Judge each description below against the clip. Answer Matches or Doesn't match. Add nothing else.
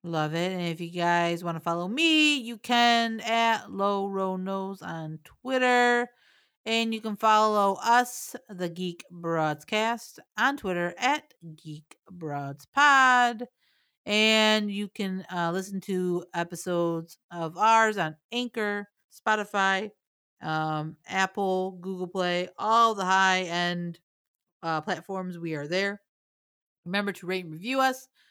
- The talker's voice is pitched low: Doesn't match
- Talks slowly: Matches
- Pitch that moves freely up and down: Doesn't match